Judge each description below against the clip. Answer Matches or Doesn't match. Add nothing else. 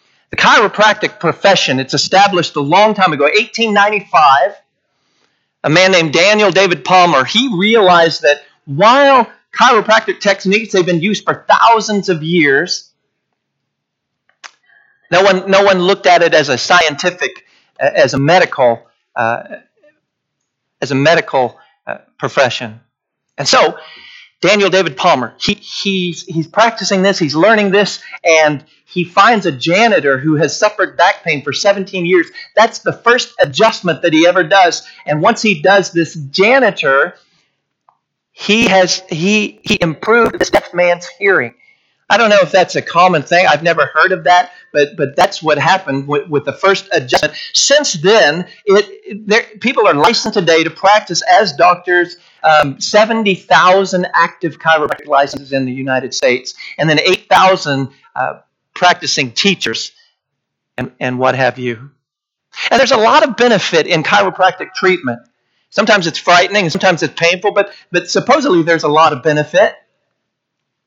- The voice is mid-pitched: Matches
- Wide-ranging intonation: Doesn't match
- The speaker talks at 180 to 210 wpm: Doesn't match